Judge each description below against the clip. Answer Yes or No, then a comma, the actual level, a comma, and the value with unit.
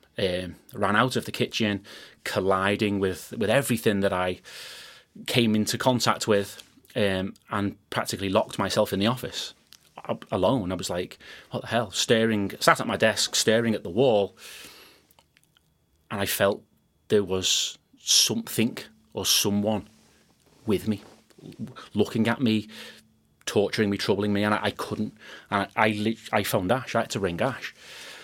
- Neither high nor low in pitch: No, low, 105 Hz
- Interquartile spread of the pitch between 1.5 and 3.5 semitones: Yes, narrow, 2.5 semitones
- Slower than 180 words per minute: Yes, average, 155 wpm